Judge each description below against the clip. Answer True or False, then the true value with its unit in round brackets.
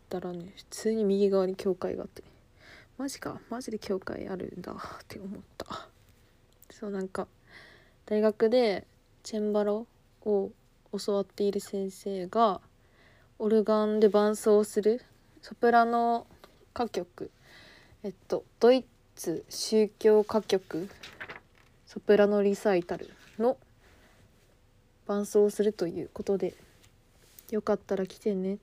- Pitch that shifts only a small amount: True (2.3 semitones)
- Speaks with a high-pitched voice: True (205 Hz)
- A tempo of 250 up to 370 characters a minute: False (230 characters per minute)